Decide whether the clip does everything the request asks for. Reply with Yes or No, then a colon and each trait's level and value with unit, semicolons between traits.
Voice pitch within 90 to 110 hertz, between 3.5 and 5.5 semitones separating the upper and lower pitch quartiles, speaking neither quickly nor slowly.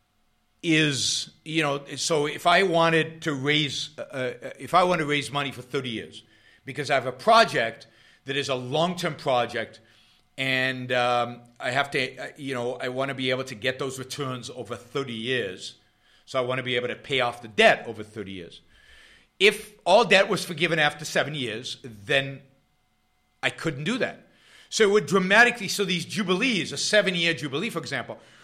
No: medium, 140 Hz; average, 5.2 semitones; average, 185 wpm